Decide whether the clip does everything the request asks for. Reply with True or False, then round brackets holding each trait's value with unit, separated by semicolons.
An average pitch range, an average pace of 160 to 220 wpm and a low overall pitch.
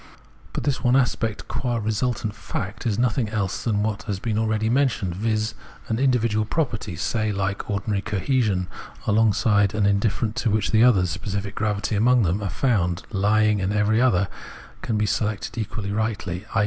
False (2.1 semitones; 170 wpm; 110 Hz)